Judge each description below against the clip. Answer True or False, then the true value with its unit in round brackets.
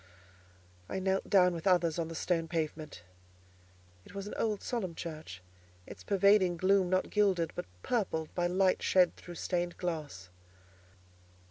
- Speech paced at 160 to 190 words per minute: False (145 wpm)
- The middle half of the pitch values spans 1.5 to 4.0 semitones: True (2.7 semitones)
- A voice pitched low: False (180 Hz)